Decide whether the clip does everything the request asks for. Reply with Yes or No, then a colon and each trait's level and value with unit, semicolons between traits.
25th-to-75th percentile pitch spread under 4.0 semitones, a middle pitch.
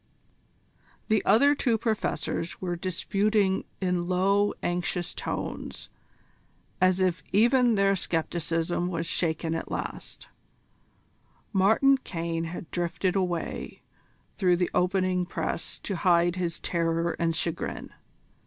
Yes: narrow, 2.6 semitones; medium, 180 Hz